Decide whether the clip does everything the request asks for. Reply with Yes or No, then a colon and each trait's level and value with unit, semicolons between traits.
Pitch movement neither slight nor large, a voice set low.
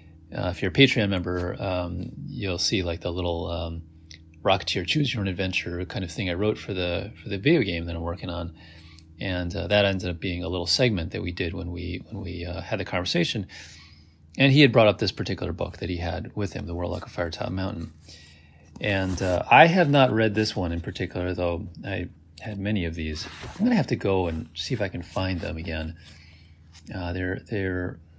Yes: average, 3.5 semitones; very low, 90 Hz